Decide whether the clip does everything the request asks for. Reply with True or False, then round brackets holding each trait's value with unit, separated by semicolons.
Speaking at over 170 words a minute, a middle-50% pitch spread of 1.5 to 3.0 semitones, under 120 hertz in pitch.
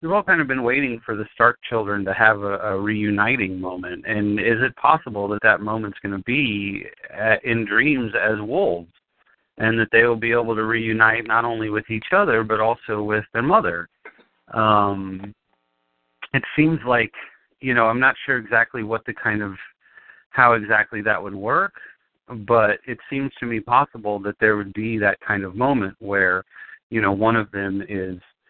True (185 wpm; 2.5 semitones; 110 Hz)